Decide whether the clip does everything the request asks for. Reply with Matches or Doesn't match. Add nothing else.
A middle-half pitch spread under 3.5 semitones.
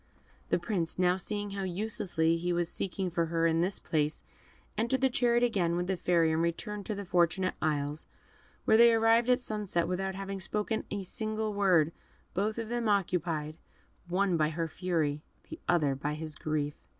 Doesn't match